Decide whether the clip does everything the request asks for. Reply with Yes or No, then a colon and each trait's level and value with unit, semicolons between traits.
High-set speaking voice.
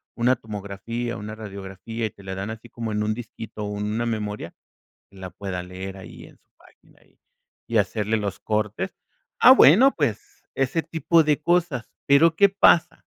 No: low, 110 Hz